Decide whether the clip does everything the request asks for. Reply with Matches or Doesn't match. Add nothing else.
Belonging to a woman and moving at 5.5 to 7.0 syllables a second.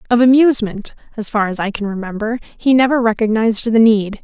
Matches